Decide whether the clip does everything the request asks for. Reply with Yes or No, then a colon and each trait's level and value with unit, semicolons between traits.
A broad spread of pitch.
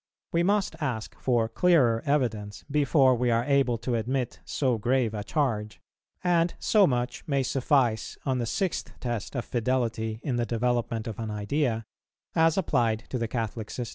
No: average, 3.5 semitones